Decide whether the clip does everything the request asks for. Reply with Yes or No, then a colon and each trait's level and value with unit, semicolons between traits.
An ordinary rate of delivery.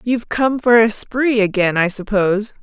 Yes: average, 185 wpm